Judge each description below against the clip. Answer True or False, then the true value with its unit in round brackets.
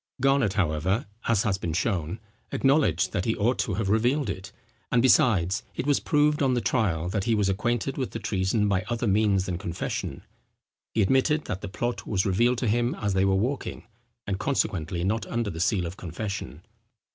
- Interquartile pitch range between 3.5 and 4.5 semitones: True (4.2 semitones)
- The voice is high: False (105 Hz)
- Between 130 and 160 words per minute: False (190 wpm)